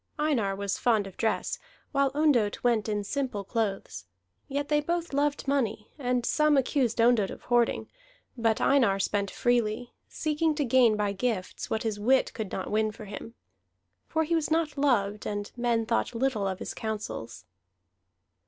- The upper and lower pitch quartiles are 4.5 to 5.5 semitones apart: Yes, average, 5.1 semitones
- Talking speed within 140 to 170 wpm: Yes, average, 165 wpm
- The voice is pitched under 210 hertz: No, high, 235 Hz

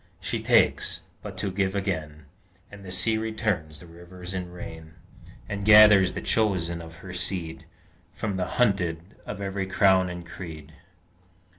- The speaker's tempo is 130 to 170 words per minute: Yes, average, 150 wpm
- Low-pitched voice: Yes, very low, 90 Hz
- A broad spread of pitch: No, average, 3.0 semitones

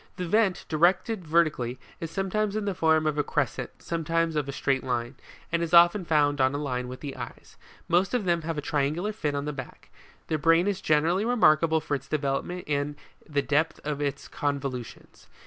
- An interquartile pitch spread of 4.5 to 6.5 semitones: No, average, 3.4 semitones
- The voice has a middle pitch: Yes, medium, 155 Hz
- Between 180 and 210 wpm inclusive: Yes, average, 200 wpm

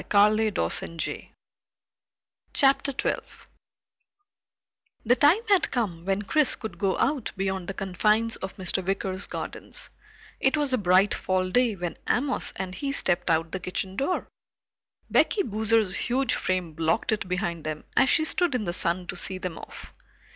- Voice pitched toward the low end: No, high, 195 Hz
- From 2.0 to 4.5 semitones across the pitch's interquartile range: No, average, 5.2 semitones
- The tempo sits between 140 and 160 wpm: Yes, average, 150 wpm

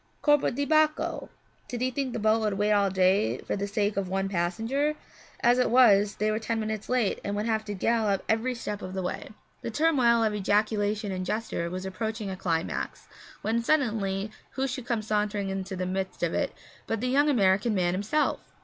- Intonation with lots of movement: No, average, 3.4 semitones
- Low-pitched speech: No, high, 215 Hz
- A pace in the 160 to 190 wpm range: No, fast, 205 wpm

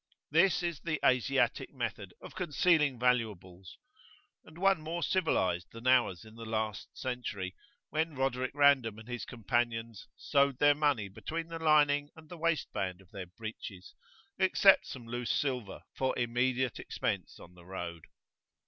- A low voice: Yes, low, 125 Hz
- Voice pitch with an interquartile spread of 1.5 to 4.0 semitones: No, average, 5.3 semitones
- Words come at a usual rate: Yes, average, 150 wpm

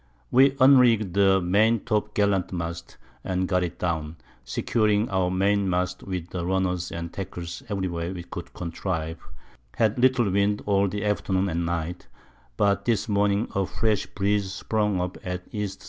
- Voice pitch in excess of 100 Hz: No, very low, 95 Hz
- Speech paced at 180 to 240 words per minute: No, average, 160 wpm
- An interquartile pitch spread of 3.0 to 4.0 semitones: No, narrow, 2.6 semitones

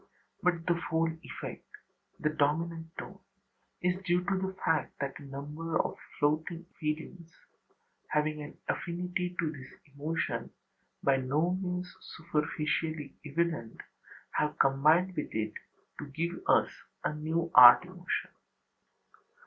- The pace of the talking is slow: Yes, slow, 125 wpm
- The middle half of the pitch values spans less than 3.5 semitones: Yes, average, 2.8 semitones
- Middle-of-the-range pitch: Yes, medium, 160 Hz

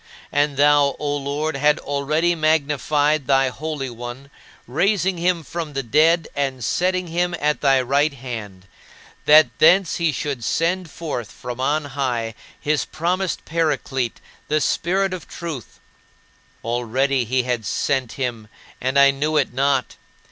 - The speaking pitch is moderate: Yes, medium, 145 Hz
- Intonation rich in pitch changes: No, average, 3.4 semitones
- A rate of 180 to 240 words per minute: No, average, 140 wpm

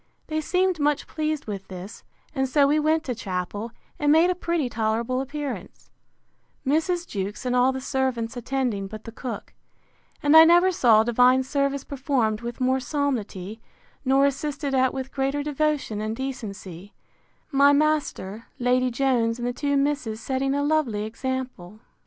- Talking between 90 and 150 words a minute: No, average, 160 wpm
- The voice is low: No, very high, 260 Hz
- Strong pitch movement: No, average, 4.2 semitones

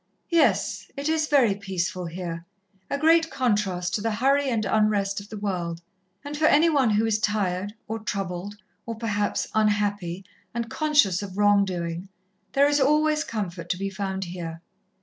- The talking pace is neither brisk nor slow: Yes, average, 170 wpm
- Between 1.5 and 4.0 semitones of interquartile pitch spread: No, wide, 5.5 semitones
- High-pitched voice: Yes, high, 205 Hz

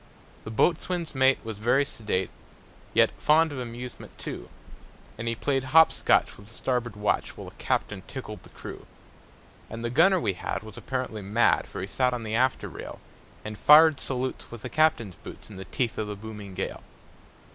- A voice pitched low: Yes, low, 120 Hz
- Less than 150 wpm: No, average, 190 wpm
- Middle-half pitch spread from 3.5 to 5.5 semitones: Yes, average, 3.9 semitones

